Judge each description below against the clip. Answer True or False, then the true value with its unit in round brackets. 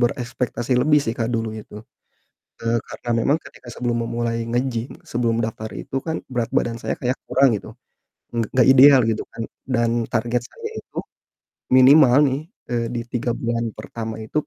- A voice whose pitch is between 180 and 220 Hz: False (120 Hz)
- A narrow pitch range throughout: True (1.8 semitones)